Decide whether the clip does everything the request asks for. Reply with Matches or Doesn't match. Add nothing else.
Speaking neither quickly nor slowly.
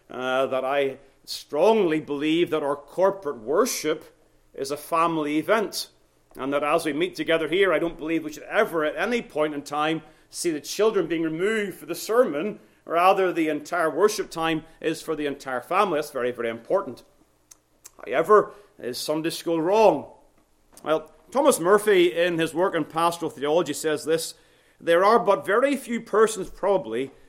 Matches